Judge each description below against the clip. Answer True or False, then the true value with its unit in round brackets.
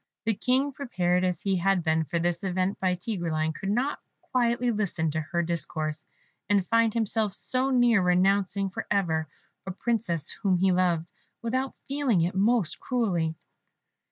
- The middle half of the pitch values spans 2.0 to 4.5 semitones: False (5.0 semitones)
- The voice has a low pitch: False (190 Hz)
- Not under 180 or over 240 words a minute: False (155 wpm)